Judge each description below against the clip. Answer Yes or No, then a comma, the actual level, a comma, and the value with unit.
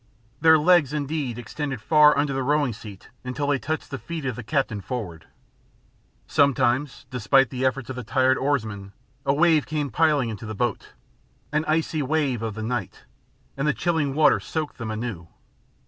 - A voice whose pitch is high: No, low, 135 Hz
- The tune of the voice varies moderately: Yes, average, 4.2 semitones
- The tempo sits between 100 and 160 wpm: No, average, 175 wpm